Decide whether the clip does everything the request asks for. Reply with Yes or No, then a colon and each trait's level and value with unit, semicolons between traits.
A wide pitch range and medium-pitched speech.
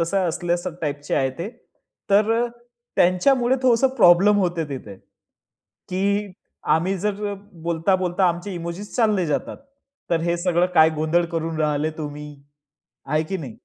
No: average, 3.7 semitones; medium, 175 Hz